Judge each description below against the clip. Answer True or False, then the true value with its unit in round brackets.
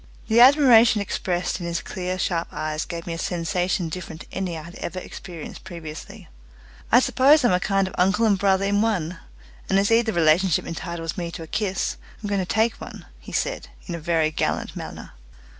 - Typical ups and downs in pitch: True (3.4 semitones)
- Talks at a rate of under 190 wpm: False (200 wpm)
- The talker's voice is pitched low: False (185 Hz)